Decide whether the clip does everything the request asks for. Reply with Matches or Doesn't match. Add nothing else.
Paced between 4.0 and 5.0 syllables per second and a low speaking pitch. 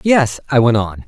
Matches